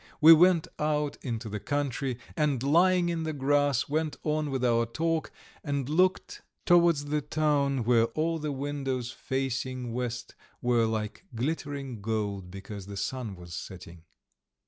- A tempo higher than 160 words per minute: No, average, 145 wpm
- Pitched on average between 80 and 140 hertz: Yes, low, 135 Hz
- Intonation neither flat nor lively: Yes, average, 4.6 semitones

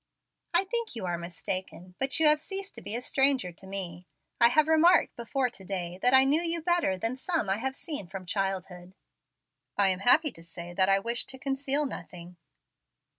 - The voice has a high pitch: Yes, high, 235 Hz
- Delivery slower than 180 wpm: No, average, 200 wpm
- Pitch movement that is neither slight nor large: No, wide, 7.9 semitones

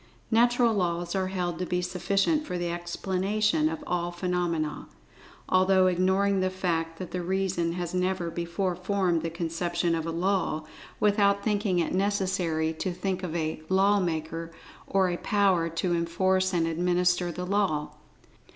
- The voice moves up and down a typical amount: No, narrow, 2.2 semitones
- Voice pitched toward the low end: No, medium, 180 Hz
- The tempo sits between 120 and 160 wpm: Yes, average, 155 wpm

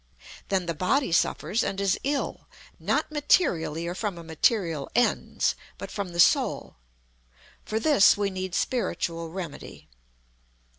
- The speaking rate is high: No, slow, 135 wpm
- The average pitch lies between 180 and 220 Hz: Yes, medium, 185 Hz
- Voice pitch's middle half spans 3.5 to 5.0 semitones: Yes, average, 4.7 semitones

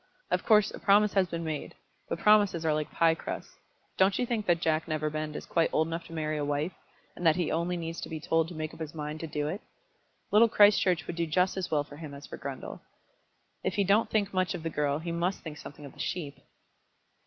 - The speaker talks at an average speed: No, fast, 240 wpm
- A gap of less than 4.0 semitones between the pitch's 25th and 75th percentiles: Yes, average, 3.2 semitones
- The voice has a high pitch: No, medium, 165 Hz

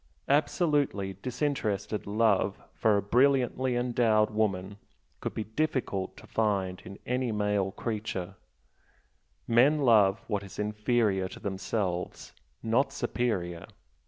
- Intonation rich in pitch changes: No, average, 3.9 semitones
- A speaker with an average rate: No, slow, 110 wpm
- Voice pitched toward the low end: Yes, low, 110 Hz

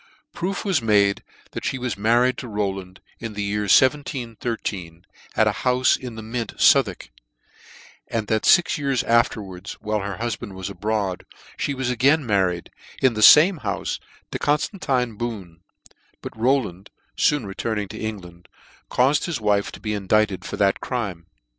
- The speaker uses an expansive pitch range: No, average, 4.2 semitones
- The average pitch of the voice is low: Yes, low, 110 Hz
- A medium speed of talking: Yes, average, 160 wpm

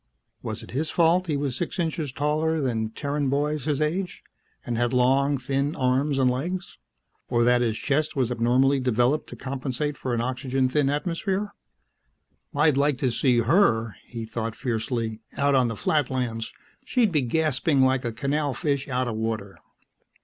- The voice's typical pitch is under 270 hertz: Yes, low, 135 Hz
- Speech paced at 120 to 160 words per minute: No, average, 170 wpm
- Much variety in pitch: No, average, 3.5 semitones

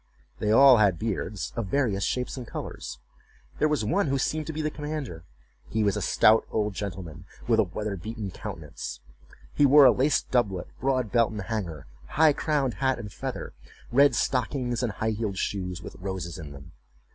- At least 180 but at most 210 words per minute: Yes, average, 185 wpm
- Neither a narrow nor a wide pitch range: No, wide, 5.7 semitones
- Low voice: Yes, low, 110 Hz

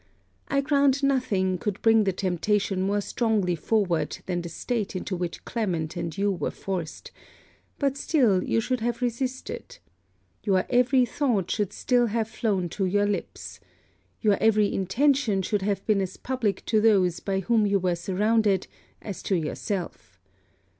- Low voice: No, high, 205 Hz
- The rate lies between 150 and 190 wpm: Yes, average, 155 wpm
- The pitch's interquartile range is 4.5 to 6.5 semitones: No, average, 3.9 semitones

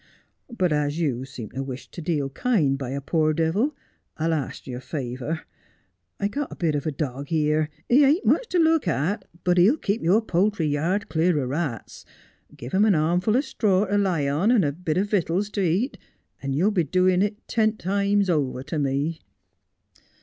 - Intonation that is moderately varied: No, wide, 5.9 semitones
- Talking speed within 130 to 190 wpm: No, average, 200 wpm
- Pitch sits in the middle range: Yes, medium, 170 Hz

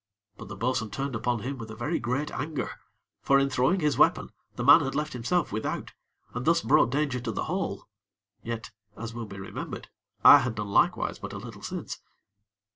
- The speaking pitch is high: No, low, 125 Hz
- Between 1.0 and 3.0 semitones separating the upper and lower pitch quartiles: No, average, 4.0 semitones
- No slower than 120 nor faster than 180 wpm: No, average, 200 wpm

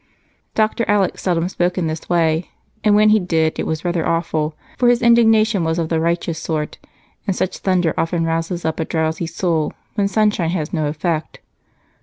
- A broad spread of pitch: No, average, 3.3 semitones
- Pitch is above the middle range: No, medium, 170 Hz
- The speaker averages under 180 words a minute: No, average, 185 wpm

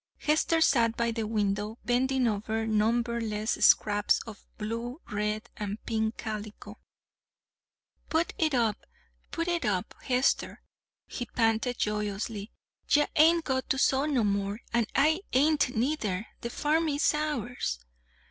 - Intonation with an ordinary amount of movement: Yes, average, 4.6 semitones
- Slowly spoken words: Yes, slow, 130 wpm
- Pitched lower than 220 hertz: No, high, 235 Hz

